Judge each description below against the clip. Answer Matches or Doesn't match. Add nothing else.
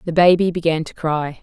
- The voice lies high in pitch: Doesn't match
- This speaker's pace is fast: Matches